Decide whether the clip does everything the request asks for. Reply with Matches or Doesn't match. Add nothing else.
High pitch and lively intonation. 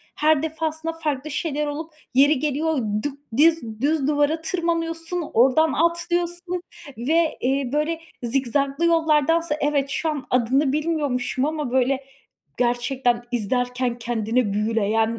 Doesn't match